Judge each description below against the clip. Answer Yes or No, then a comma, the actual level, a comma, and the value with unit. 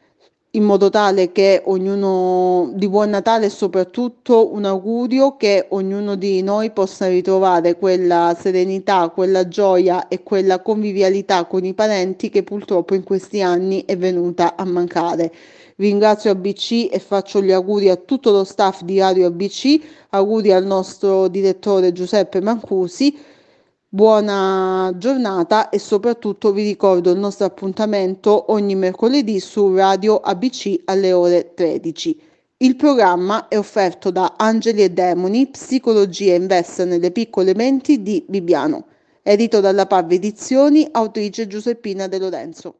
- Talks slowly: No, average, 135 wpm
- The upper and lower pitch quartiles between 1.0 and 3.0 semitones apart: Yes, narrow, 2.4 semitones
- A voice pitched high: Yes, high, 195 Hz